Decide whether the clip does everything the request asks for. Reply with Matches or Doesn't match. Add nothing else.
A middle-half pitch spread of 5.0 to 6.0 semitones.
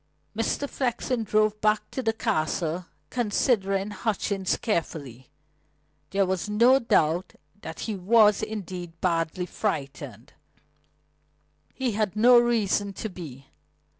Matches